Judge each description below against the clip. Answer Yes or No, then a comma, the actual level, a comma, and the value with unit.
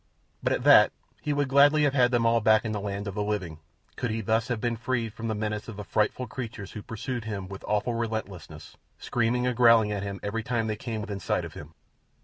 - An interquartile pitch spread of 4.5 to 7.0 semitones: No, narrow, 2.5 semitones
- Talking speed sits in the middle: No, fast, 240 wpm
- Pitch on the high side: No, low, 110 Hz